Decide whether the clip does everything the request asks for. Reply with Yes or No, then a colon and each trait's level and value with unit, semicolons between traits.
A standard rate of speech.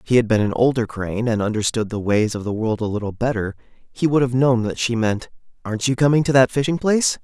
No: fast, 255 wpm